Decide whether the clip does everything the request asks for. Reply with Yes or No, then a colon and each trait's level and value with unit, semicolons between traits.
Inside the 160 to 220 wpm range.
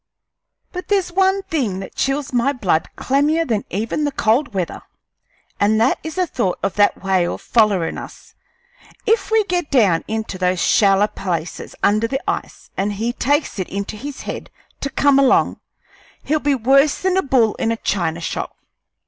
Yes: average, 175 wpm